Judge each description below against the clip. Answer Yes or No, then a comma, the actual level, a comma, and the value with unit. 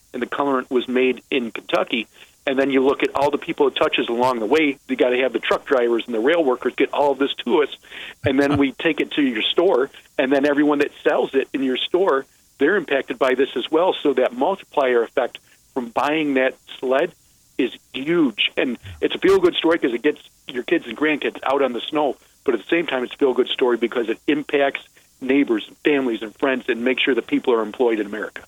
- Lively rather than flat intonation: Yes, wide, 5.7 semitones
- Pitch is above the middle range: No, medium, 140 Hz